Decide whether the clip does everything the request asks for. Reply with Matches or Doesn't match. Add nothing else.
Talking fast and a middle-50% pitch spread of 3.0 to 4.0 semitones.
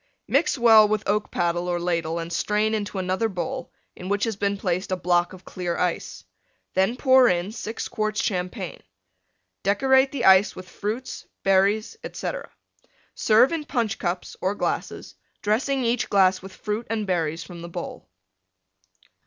Doesn't match